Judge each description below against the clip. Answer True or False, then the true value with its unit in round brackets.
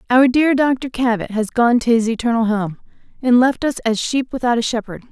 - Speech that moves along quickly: True (210 wpm)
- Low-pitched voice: False (240 Hz)